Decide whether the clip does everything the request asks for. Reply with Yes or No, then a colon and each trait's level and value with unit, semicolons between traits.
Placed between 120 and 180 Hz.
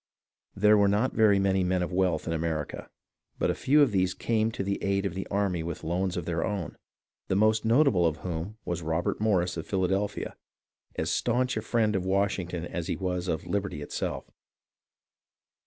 No: very low, 95 Hz